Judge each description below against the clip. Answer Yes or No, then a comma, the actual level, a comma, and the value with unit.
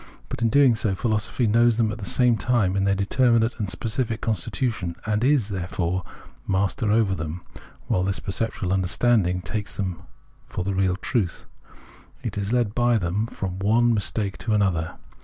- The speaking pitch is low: Yes, low, 105 Hz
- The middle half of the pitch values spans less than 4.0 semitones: Yes, average, 3.5 semitones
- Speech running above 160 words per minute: Yes, average, 170 wpm